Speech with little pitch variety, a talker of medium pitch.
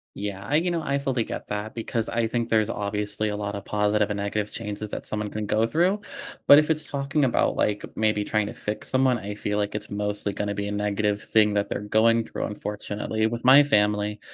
No: narrow, 2.1 semitones; low, 105 Hz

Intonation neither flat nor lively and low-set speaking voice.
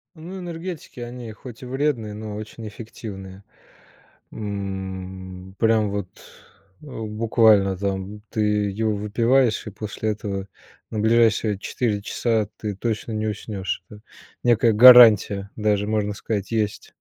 No: narrow, 2.2 semitones; low, 105 Hz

